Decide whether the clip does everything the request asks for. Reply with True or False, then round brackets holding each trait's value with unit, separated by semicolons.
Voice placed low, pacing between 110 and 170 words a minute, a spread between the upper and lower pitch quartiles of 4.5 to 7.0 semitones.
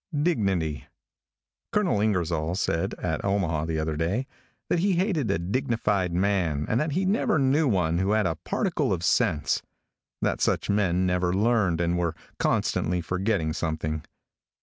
True (95 Hz; 150 wpm; 5.2 semitones)